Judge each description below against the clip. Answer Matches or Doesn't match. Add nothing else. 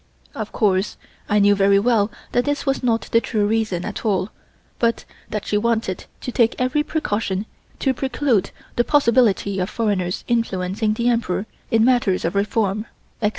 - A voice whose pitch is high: Matches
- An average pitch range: Matches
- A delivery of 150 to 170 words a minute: Matches